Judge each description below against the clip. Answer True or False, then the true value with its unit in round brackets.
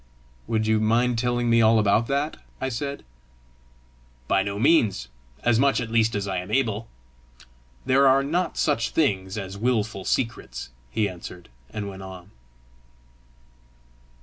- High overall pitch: False (110 Hz)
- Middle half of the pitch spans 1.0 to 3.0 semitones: False (3.8 semitones)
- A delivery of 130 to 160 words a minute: True (145 wpm)